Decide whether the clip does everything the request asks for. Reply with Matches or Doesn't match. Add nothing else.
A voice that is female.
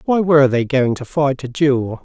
Doesn't match